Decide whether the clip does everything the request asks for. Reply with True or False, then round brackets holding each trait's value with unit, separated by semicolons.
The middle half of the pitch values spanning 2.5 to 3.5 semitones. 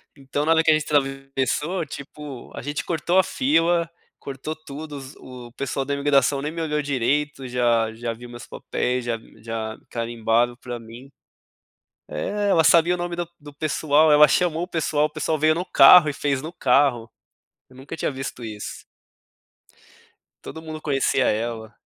False (4.1 semitones)